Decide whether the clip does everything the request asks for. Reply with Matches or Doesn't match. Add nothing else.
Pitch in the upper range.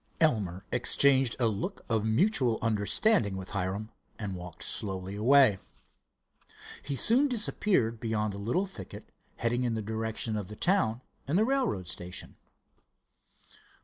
Doesn't match